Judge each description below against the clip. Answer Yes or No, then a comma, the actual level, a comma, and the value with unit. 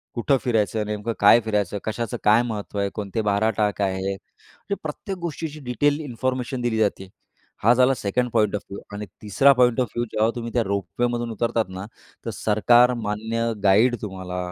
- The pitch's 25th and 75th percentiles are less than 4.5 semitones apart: Yes, average, 3.0 semitones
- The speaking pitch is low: Yes, low, 110 Hz